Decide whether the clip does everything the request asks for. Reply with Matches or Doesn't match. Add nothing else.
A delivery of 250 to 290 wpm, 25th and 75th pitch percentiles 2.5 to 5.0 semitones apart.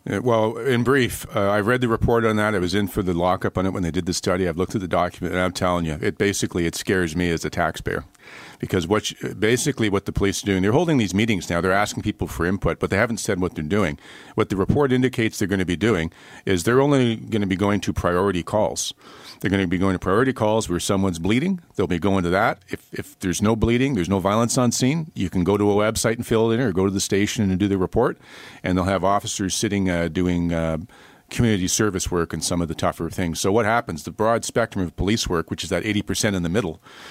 Matches